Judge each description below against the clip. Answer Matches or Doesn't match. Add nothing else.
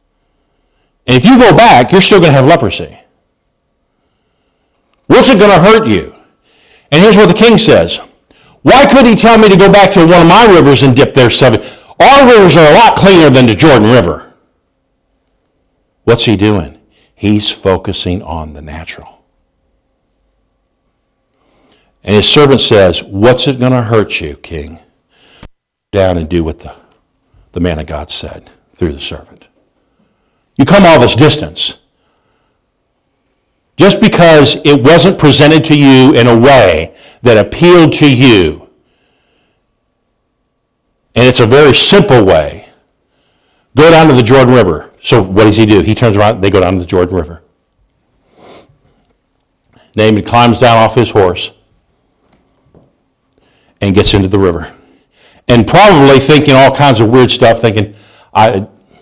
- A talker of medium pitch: Doesn't match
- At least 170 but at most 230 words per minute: Doesn't match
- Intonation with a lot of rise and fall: Matches